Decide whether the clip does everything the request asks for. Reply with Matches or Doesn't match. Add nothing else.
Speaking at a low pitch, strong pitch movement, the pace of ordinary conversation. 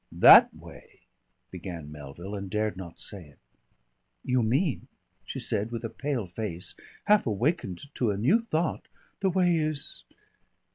Matches